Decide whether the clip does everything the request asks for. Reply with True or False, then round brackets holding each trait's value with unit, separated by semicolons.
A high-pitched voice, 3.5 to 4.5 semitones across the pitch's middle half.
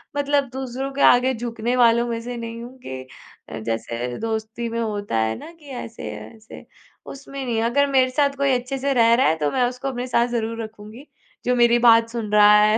False (235 Hz; 2.7 semitones)